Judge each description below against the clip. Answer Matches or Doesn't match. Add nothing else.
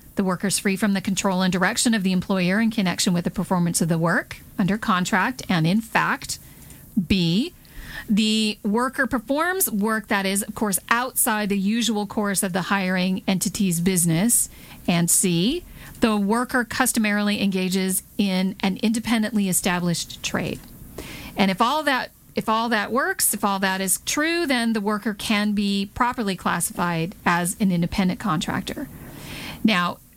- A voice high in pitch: Matches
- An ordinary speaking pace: Matches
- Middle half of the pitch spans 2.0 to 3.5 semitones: Matches